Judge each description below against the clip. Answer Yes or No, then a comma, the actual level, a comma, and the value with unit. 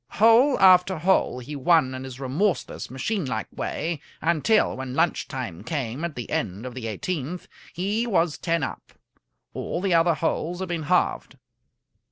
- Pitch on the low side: No, medium, 165 Hz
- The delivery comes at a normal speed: Yes, average, 165 wpm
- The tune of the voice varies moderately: No, wide, 5.7 semitones